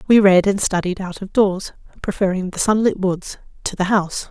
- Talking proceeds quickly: No, average, 195 wpm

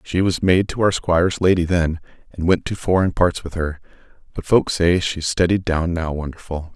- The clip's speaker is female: No, male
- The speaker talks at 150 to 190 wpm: No, fast, 205 wpm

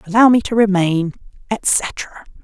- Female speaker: Yes, female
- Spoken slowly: Yes, slow, 125 wpm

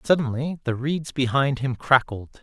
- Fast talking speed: No, average, 150 wpm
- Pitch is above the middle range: No, low, 135 Hz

